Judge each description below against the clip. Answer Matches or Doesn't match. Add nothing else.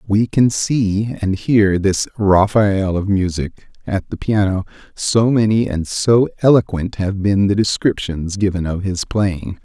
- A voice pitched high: Doesn't match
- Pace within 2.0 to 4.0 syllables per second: Matches